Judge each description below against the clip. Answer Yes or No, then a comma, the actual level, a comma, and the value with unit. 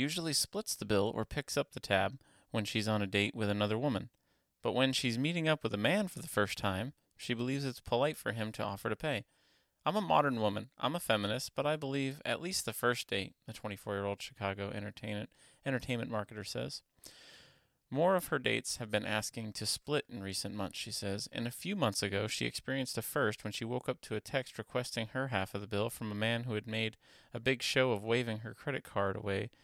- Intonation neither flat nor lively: Yes, average, 4.2 semitones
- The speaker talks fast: Yes, fast, 225 wpm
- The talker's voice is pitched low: Yes, low, 115 Hz